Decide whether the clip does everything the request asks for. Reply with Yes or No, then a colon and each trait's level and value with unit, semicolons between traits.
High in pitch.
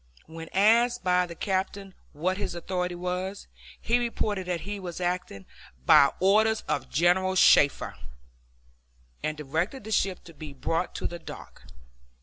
No: medium, 180 Hz